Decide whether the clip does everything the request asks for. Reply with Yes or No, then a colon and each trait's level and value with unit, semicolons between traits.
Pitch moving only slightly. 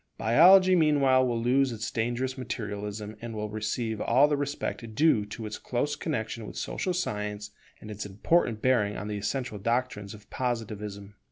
No: average, 3.8 semitones